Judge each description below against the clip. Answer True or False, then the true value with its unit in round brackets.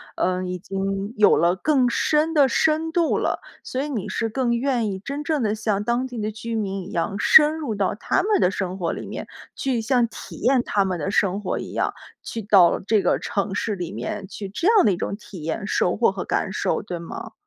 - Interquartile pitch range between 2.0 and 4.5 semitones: False (5.1 semitones)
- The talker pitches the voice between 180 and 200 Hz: False (210 Hz)